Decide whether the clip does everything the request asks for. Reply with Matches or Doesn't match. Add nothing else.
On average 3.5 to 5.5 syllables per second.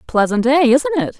Matches